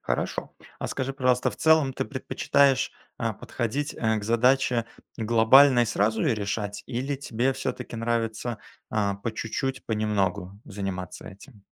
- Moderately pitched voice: No, low, 115 Hz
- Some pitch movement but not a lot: Yes, average, 3.7 semitones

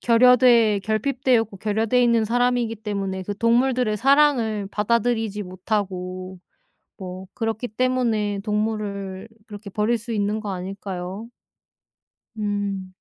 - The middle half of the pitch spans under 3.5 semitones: Yes, average, 2.8 semitones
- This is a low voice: No, high, 215 Hz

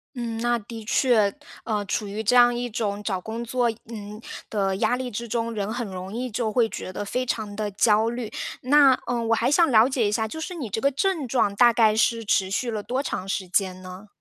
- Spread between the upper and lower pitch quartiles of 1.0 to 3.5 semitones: Yes, average, 2.9 semitones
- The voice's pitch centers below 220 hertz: No, high, 225 Hz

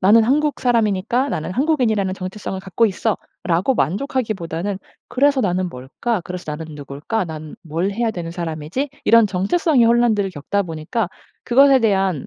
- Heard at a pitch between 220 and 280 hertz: No, high, 200 Hz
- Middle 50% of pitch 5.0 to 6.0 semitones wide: Yes, wide, 5.5 semitones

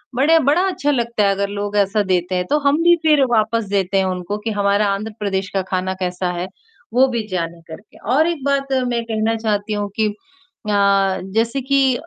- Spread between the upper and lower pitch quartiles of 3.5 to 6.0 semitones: Yes, wide, 5.5 semitones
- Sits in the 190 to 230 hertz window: Yes, high, 215 Hz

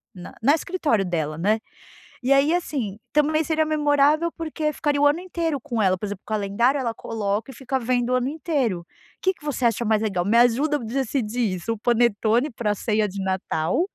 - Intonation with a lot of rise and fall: Yes, wide, 5.8 semitones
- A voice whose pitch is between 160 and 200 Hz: No, high, 245 Hz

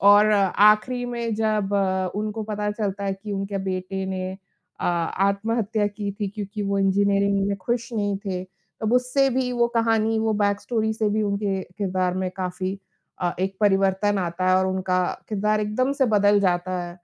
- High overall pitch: Yes, high, 200 Hz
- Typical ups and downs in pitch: No, narrow, 2.2 semitones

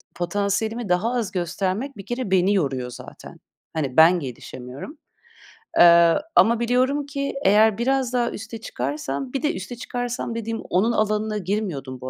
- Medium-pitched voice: No, high, 210 Hz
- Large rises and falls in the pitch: Yes, wide, 5.8 semitones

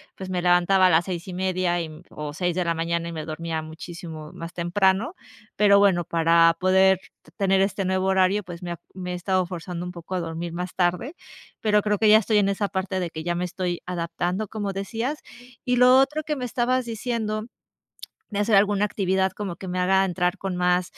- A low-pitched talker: No, medium, 185 Hz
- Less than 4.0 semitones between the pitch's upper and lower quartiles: Yes, average, 2.7 semitones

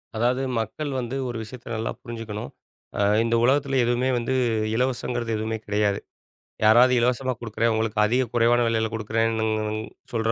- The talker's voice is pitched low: Yes, low, 115 Hz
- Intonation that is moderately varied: No, narrow, 1.8 semitones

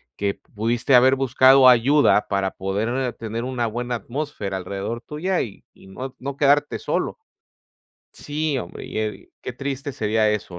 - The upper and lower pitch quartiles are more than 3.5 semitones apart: Yes, average, 4.2 semitones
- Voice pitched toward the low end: Yes, low, 120 Hz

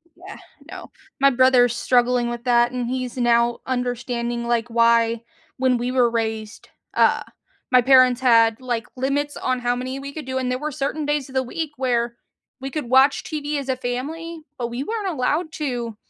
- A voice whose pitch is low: No, very high, 250 Hz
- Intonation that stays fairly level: Yes, narrow, 2.3 semitones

